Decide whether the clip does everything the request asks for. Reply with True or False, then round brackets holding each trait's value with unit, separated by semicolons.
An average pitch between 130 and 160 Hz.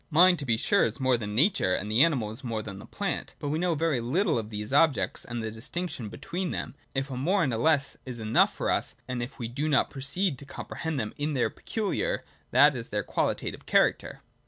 True (135 Hz)